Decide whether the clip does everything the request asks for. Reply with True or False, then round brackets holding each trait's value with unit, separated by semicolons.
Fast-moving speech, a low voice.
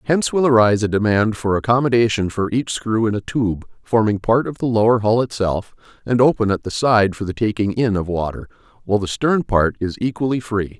True (210 wpm; 110 Hz)